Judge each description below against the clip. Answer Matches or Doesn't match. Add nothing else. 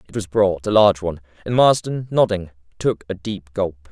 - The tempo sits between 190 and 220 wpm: Matches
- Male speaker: Matches